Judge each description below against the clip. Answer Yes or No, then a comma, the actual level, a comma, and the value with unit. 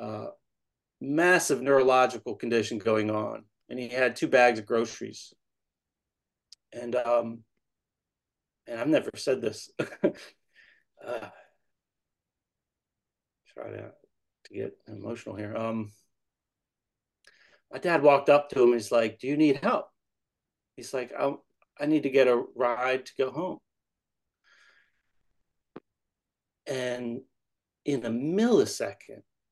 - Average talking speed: No, slow, 115 wpm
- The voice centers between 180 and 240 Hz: No, low, 120 Hz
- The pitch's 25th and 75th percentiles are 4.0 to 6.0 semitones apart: No, average, 2.8 semitones